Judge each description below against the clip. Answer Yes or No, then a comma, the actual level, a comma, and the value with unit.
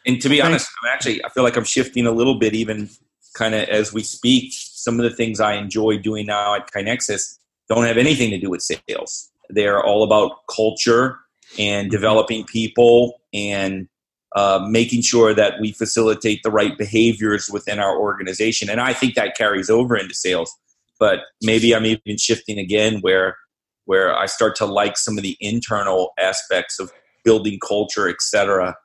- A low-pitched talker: Yes, low, 110 Hz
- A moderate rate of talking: Yes, average, 180 wpm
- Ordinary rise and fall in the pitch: No, narrow, 2.1 semitones